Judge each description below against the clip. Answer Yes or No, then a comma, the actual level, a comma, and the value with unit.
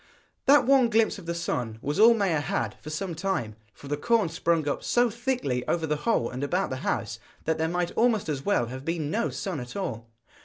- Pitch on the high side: No, medium, 165 Hz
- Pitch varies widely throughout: Yes, wide, 7.1 semitones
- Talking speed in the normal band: No, fast, 225 wpm